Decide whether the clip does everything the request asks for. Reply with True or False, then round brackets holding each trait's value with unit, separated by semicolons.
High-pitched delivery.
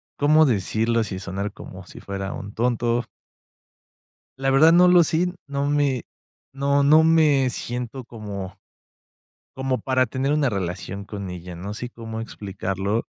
False (120 Hz)